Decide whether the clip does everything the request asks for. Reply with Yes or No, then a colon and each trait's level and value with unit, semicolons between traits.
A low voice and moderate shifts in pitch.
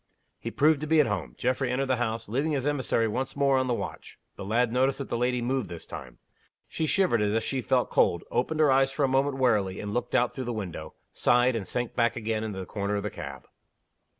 Yes: low, 125 Hz; average, 3.9 semitones